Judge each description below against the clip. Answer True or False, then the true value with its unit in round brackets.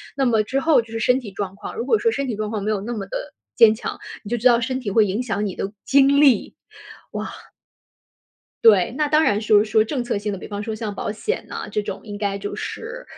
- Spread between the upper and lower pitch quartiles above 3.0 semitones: True (3.9 semitones)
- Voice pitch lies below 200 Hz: False (220 Hz)